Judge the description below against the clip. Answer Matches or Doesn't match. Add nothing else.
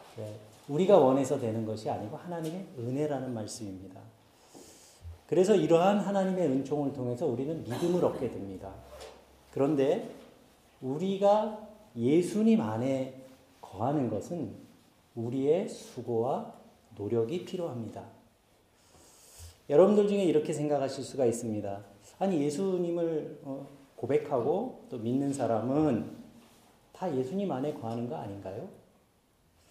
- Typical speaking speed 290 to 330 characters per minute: Doesn't match